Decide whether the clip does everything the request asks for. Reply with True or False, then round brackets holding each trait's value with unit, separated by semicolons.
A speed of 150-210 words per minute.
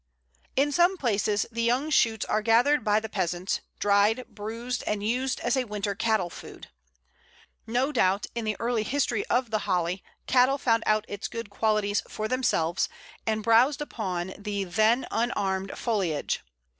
True (155 wpm)